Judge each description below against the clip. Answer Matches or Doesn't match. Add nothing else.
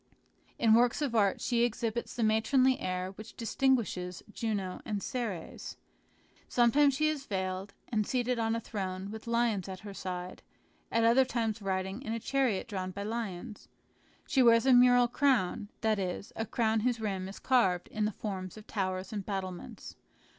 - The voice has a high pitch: Matches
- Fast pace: Doesn't match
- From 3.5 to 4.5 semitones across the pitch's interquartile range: Matches